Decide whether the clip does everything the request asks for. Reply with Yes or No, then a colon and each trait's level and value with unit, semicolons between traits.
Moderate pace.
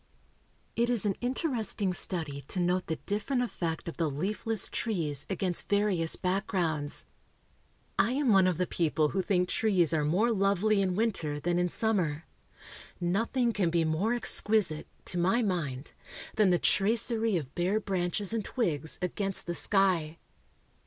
Yes: average, 150 wpm